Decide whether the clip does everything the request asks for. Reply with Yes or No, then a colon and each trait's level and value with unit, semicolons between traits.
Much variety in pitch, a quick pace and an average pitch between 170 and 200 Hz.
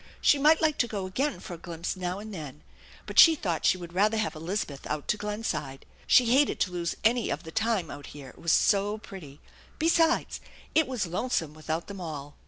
Yes: wide, 5.8 semitones; fast, 215 wpm; high, 190 Hz